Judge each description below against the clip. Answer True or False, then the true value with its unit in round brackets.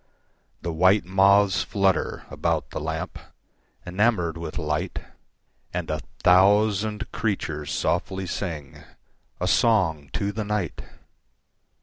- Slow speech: True (90 wpm)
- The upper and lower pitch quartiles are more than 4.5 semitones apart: False (3.8 semitones)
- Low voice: True (95 Hz)